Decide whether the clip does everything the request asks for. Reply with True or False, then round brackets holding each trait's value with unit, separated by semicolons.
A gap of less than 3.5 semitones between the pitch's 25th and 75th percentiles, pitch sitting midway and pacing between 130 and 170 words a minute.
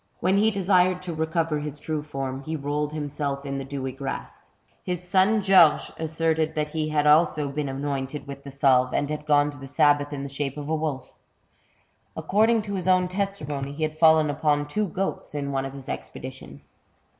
False (2.9 semitones; 150 Hz; 195 wpm)